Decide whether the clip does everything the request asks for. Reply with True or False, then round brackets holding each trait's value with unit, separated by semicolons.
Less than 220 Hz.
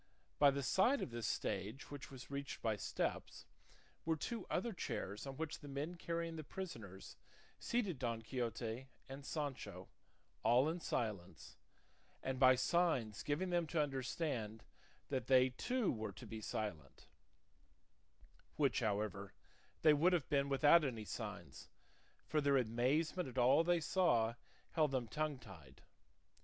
True (135 Hz)